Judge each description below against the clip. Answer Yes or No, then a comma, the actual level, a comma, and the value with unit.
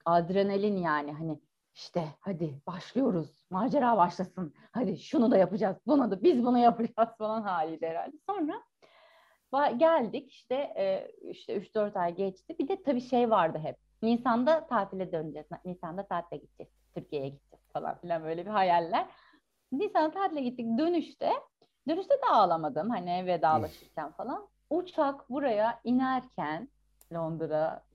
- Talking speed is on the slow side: No, average, 130 wpm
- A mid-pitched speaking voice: No, high, 220 Hz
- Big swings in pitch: Yes, wide, 8.8 semitones